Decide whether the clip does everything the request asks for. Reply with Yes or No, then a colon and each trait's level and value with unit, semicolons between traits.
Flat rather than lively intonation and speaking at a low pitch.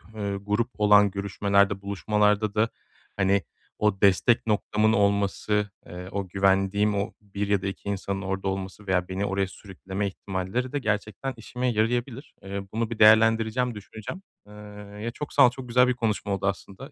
Yes: narrow, 2.1 semitones; low, 105 Hz